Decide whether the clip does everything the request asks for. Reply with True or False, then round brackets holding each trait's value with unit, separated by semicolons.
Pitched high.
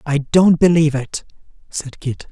False (150 Hz)